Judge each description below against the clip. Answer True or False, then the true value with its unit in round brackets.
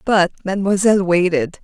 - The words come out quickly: False (110 wpm)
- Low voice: False (185 Hz)